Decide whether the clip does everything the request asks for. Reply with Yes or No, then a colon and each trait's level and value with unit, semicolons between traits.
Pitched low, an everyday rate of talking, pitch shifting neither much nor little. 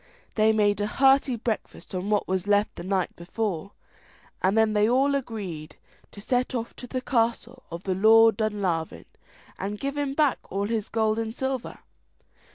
No: high, 220 Hz; average, 175 wpm; average, 3.5 semitones